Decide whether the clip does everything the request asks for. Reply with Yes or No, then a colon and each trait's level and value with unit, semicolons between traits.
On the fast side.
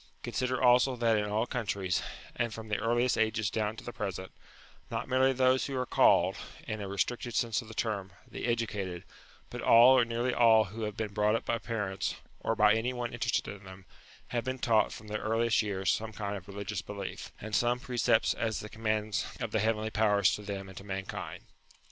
Yes: fast, 210 wpm